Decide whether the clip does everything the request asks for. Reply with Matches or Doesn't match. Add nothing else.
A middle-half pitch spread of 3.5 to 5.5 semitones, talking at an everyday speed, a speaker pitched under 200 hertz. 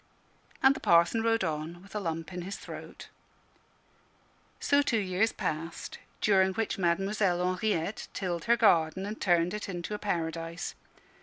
Matches